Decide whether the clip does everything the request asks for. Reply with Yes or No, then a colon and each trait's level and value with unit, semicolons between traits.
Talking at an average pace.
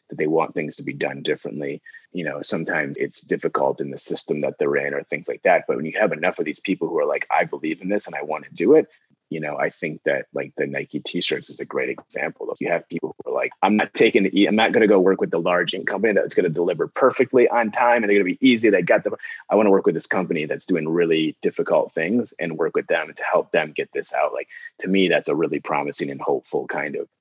No: fast, 280 wpm